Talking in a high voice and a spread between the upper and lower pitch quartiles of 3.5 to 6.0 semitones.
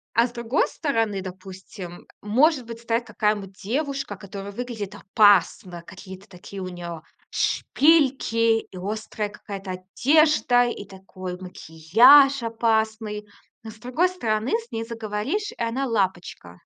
Yes: high, 220 Hz; average, 4.1 semitones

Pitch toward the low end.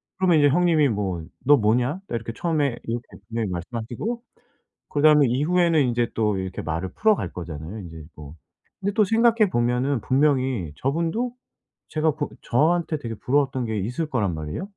Yes: low, 130 Hz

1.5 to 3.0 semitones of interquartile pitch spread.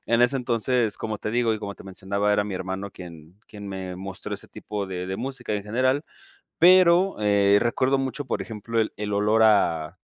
No: average, 3.8 semitones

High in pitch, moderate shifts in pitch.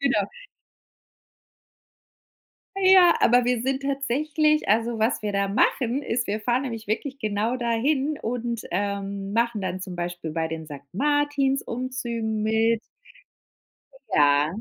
Yes: high, 230 Hz; average, 4.9 semitones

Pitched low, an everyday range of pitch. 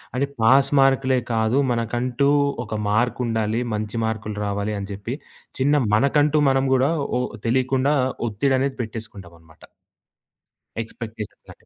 Yes: low, 120 Hz; average, 3.7 semitones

